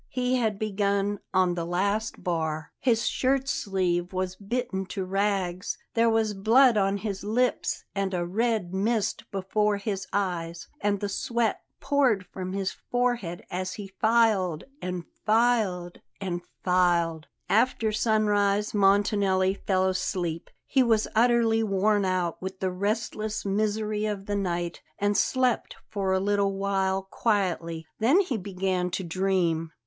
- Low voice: No, high, 200 Hz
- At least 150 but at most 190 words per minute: No, average, 140 wpm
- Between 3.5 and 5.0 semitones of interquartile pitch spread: No, average, 2.7 semitones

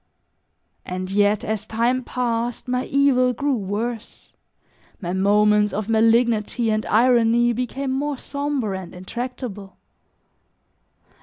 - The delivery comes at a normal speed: No, slow, 105 wpm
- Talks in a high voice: Yes, high, 230 Hz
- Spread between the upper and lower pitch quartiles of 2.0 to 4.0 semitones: Yes, average, 3.3 semitones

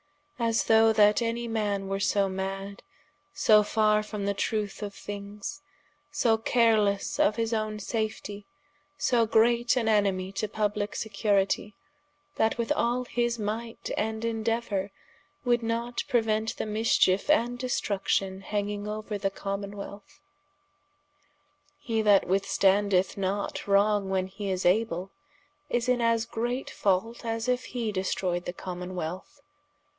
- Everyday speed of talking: No, slow, 130 wpm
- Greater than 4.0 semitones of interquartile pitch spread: No, narrow, 2.5 semitones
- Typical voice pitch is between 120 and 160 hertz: No, high, 210 Hz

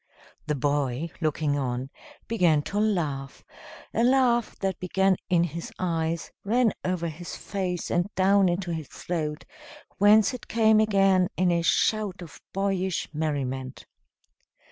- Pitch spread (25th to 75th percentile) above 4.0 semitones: Yes, average, 4.4 semitones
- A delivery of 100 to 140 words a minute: Yes, slow, 135 wpm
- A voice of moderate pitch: Yes, medium, 175 Hz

